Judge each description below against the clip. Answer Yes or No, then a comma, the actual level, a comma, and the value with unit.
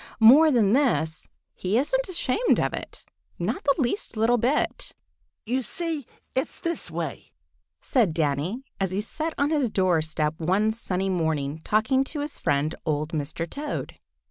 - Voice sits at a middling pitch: No, high, 220 Hz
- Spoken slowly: No, average, 150 wpm